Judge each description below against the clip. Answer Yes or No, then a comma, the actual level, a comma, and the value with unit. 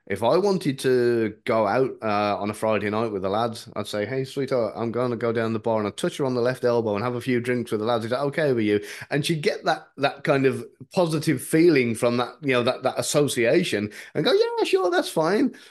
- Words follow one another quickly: Yes, fast, 260 wpm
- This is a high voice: No, low, 125 Hz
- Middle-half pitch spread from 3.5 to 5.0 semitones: Yes, average, 3.8 semitones